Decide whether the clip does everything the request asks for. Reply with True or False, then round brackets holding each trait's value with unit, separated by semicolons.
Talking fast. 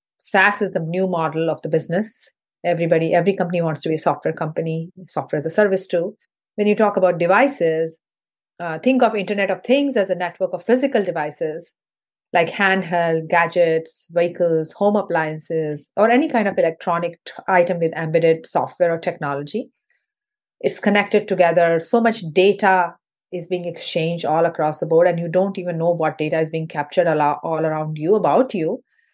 False (175 wpm)